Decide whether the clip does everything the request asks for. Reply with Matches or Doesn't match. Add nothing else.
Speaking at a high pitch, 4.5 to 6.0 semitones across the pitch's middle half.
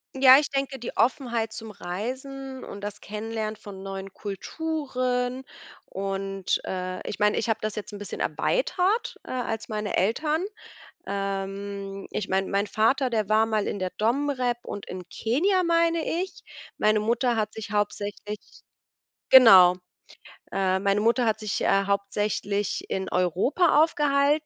Matches